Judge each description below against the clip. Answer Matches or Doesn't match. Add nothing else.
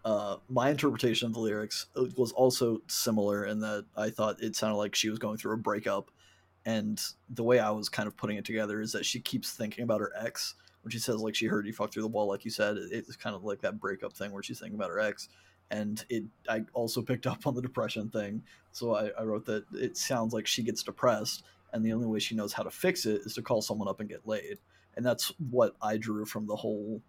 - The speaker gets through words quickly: Matches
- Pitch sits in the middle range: Doesn't match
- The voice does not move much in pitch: Matches